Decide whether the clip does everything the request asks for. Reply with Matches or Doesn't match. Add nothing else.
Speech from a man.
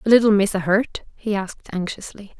Doesn't match